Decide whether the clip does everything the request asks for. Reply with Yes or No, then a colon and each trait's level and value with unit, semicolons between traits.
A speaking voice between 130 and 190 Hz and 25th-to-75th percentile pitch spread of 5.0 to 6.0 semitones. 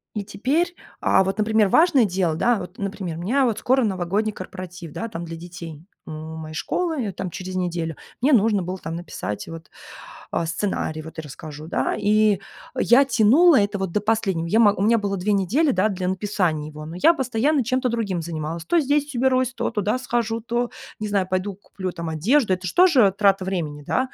No: high, 200 Hz; average, 5.3 semitones